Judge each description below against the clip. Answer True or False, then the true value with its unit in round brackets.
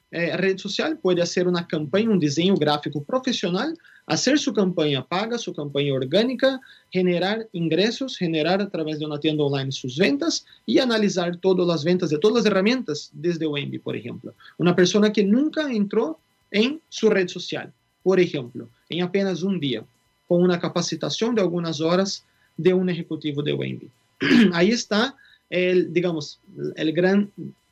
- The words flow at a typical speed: True (160 wpm)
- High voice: False (180 Hz)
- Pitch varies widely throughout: False (4.8 semitones)